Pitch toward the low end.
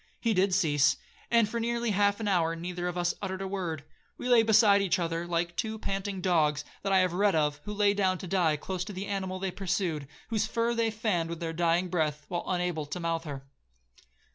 No: medium, 185 Hz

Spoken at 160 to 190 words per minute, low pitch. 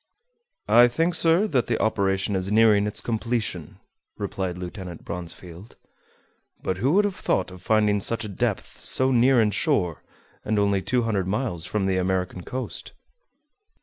No: average, 150 wpm; low, 105 Hz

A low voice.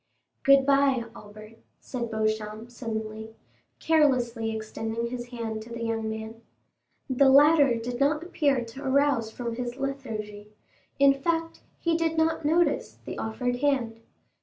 No: high, 240 Hz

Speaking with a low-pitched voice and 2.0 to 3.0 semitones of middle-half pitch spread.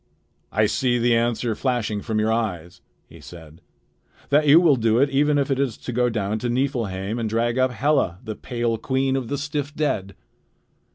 No: low, 120 Hz; average, 3.8 semitones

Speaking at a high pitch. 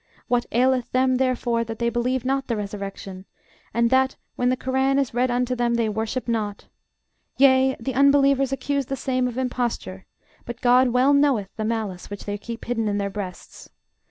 Yes: high, 245 Hz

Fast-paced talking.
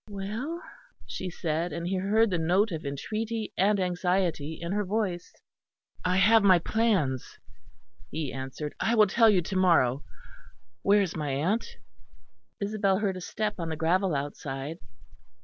No: average, 150 wpm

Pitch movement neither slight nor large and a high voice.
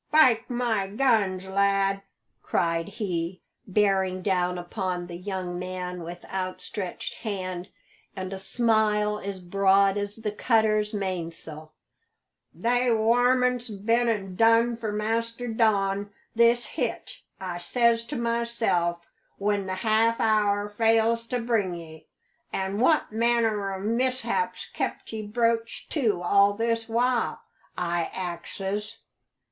Yes: average, 3.5 semitones; high, 205 Hz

